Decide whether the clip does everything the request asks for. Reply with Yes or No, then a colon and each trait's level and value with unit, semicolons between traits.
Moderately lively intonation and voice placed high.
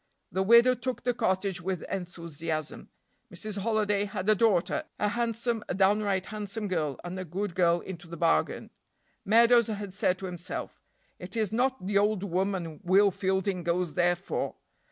Yes: average, 3.2 semitones; high, 195 Hz